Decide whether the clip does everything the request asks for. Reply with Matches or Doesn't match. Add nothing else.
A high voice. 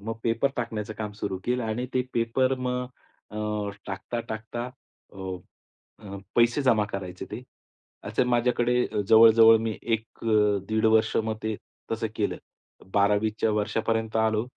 Doesn't match